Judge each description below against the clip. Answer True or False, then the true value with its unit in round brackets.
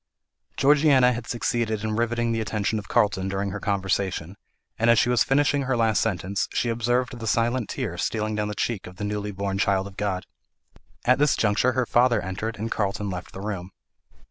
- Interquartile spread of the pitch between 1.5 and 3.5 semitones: True (3.2 semitones)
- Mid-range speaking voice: False (110 Hz)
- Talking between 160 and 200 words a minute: True (195 wpm)